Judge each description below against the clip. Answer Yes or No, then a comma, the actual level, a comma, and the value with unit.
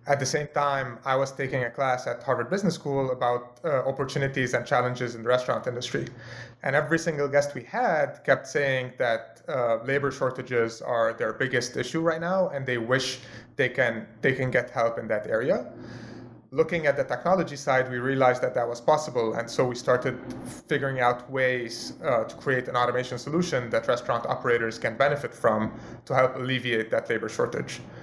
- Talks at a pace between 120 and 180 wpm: No, average, 190 wpm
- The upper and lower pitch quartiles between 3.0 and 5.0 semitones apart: No, narrow, 2.5 semitones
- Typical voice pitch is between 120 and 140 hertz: Yes, low, 130 Hz